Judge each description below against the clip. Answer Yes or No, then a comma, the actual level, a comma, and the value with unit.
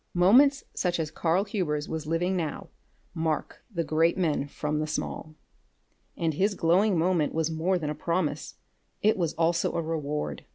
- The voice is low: No, medium, 165 Hz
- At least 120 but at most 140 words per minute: No, average, 165 wpm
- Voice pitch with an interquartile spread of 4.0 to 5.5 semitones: No, average, 2.8 semitones